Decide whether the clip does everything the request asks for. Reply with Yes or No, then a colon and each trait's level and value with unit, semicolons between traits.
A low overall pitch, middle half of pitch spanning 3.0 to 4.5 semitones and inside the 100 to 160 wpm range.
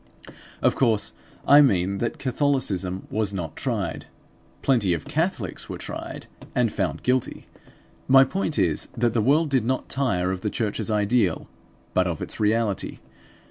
No: low, 110 Hz; wide, 5.6 semitones; average, 150 wpm